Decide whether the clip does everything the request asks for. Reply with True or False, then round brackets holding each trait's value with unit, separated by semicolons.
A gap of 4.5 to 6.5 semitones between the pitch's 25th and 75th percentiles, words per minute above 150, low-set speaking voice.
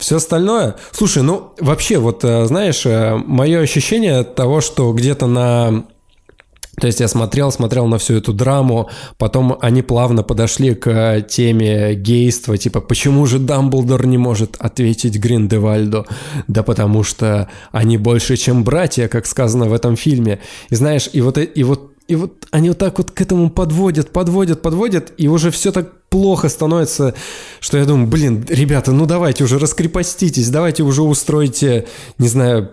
True (4.9 semitones; 160 wpm; 130 Hz)